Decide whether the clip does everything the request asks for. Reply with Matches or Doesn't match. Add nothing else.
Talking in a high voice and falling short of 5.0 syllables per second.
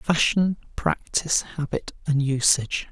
Doesn't match